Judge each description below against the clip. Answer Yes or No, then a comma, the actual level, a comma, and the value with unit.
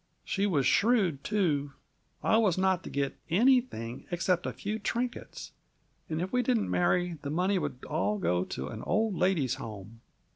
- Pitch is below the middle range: No, medium, 180 Hz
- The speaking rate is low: No, average, 170 wpm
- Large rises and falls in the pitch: Yes, wide, 6.8 semitones